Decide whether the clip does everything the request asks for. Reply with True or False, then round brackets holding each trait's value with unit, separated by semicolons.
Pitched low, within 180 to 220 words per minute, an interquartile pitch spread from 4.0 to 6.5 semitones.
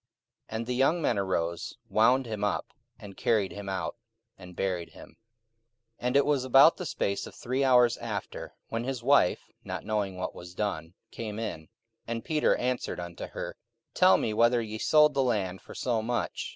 True (115 Hz; 190 wpm; 4.5 semitones)